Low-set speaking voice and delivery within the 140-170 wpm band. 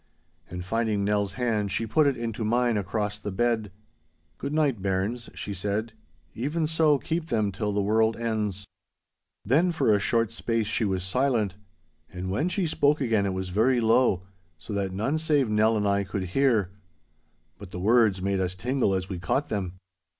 No: low, 110 Hz; average, 180 wpm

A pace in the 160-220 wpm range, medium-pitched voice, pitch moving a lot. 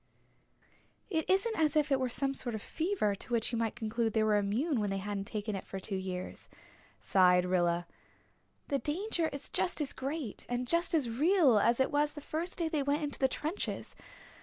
No: fast, 205 wpm; very high, 260 Hz; wide, 6.8 semitones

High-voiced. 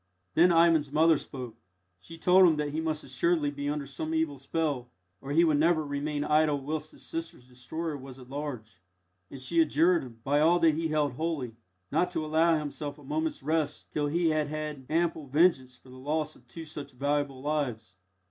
No: medium, 150 Hz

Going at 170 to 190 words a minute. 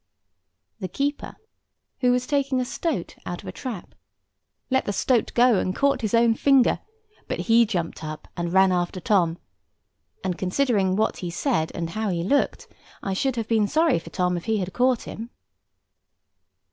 Yes: average, 175 wpm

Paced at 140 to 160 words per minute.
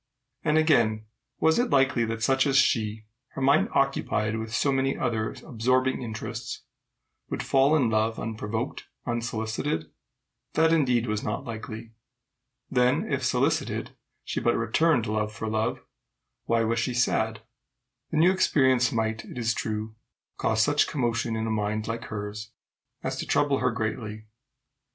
Yes: average, 150 wpm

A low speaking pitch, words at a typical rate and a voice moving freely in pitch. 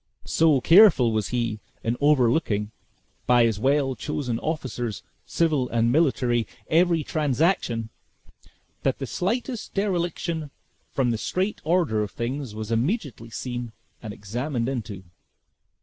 No: low, 130 Hz; slow, 120 wpm; wide, 5.7 semitones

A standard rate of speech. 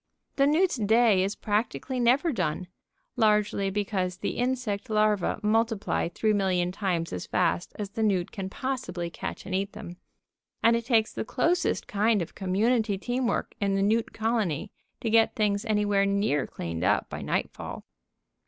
Yes: average, 160 wpm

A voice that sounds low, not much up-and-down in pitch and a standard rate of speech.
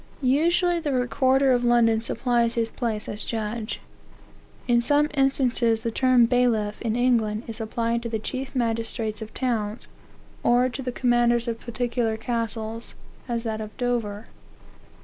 No: high, 235 Hz; narrow, 1.9 semitones; average, 150 wpm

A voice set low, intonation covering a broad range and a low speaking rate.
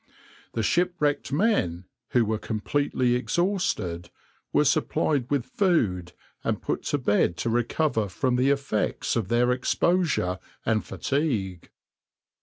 Yes: low, 125 Hz; wide, 5.8 semitones; slow, 120 wpm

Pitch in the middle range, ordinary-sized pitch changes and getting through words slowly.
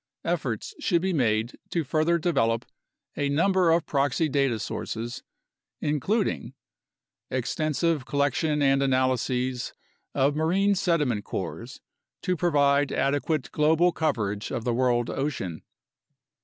Yes: medium, 145 Hz; average, 4.4 semitones; slow, 115 wpm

